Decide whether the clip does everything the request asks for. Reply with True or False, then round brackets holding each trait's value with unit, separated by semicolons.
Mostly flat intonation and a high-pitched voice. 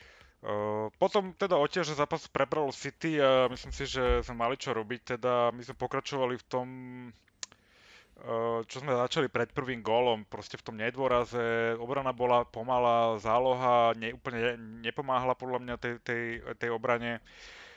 False (2.2 semitones; 125 Hz)